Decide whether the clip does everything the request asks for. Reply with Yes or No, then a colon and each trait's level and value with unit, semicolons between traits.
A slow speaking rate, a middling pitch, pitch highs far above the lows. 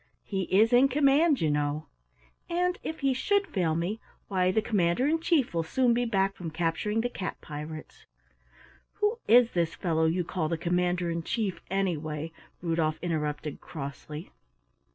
No: average, 160 wpm; medium, 180 Hz; wide, 7.1 semitones